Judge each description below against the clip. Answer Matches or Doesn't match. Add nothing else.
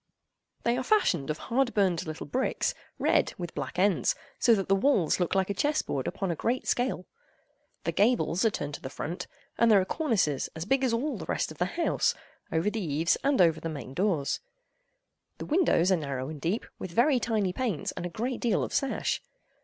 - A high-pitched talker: Matches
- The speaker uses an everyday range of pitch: Doesn't match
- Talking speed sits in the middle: Doesn't match